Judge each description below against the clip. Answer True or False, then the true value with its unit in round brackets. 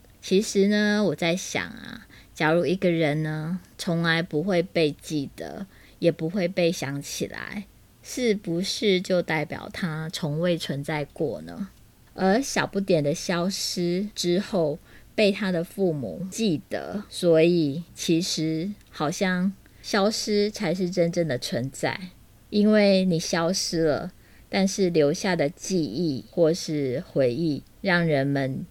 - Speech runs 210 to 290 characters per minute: False (190 characters per minute)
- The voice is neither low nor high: True (170 Hz)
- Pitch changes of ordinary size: True (3.6 semitones)